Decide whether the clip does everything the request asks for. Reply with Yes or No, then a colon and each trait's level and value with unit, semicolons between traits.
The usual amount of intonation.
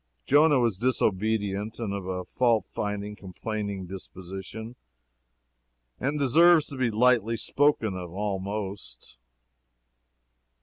Yes: average, 4.3 semitones